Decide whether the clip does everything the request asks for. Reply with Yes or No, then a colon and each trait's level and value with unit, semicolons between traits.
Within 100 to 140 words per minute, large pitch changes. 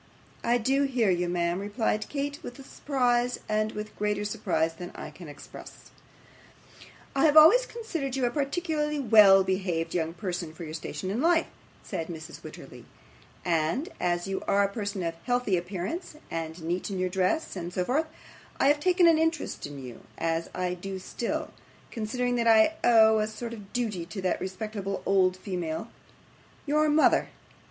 No: average, 170 wpm; wide, 6.6 semitones